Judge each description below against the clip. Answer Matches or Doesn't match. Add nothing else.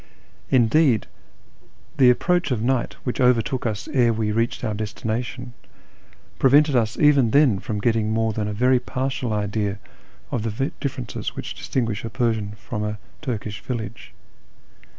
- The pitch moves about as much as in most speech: Matches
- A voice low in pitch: Matches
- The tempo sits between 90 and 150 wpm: Matches